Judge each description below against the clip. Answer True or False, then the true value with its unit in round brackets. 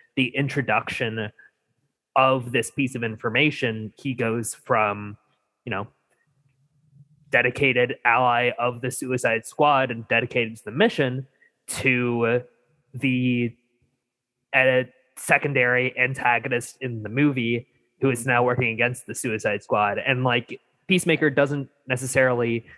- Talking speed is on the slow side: True (115 wpm)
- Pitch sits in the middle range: False (125 Hz)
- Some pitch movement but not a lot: False (2.2 semitones)